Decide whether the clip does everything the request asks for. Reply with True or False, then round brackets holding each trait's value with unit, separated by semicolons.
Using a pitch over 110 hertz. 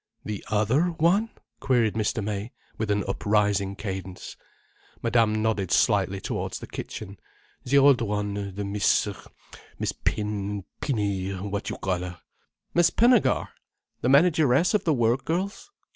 False (105 Hz)